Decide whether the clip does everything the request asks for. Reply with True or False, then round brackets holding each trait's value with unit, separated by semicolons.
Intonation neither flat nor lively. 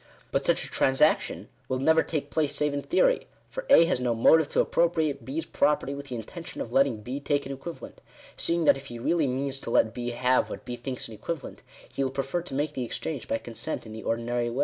True (4.4 semitones)